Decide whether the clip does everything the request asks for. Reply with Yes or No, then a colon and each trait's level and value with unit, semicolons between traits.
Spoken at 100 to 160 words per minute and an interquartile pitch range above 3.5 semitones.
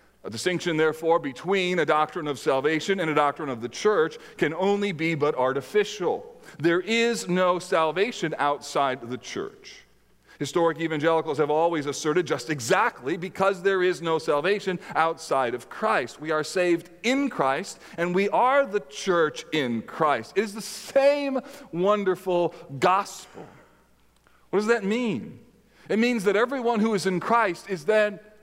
Yes: average, 155 wpm; average, 5.0 semitones